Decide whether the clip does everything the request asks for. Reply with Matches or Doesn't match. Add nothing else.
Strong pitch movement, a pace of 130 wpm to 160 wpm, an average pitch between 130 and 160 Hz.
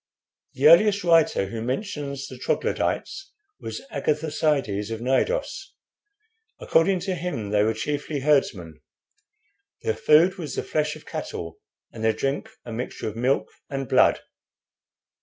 Matches